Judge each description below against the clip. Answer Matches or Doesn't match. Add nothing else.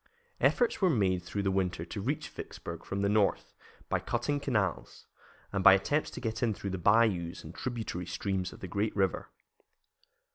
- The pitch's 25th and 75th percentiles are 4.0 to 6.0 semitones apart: Doesn't match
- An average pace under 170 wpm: Doesn't match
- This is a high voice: Doesn't match